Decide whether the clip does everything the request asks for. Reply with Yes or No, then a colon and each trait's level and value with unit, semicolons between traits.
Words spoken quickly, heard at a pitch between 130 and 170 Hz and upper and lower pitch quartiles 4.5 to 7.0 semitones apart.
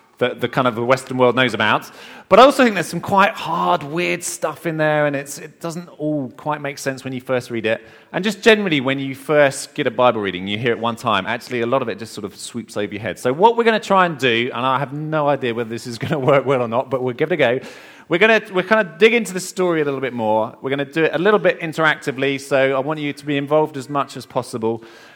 Yes: fast, 280 wpm; medium, 140 Hz; average, 5.0 semitones